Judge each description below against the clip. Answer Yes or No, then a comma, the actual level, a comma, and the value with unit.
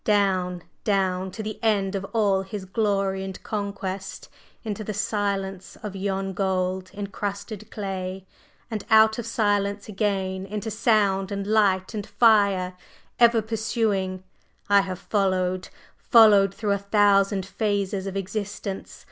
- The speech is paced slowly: Yes, slow, 130 wpm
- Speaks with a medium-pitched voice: No, high, 200 Hz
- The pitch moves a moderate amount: No, narrow, 1.8 semitones